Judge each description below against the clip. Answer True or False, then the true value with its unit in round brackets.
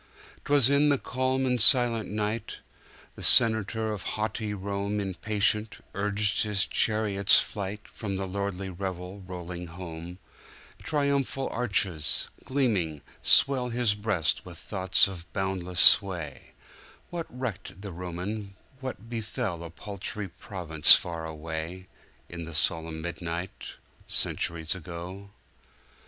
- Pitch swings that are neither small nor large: True (3.9 semitones)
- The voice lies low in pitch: True (100 Hz)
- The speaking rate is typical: False (110 wpm)